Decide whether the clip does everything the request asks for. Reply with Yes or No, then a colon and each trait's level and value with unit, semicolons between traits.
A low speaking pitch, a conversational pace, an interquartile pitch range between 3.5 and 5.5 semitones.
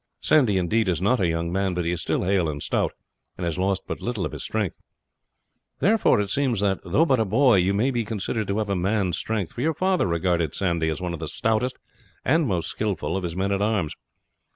No: low, 100 Hz; fast, 235 wpm; average, 4.2 semitones